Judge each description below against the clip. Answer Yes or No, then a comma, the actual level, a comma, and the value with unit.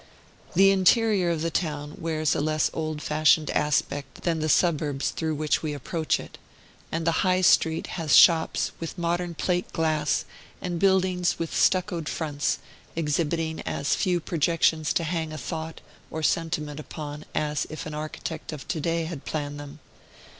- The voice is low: No, medium, 160 Hz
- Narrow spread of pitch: Yes, narrow, 2.0 semitones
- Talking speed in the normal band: Yes, average, 160 wpm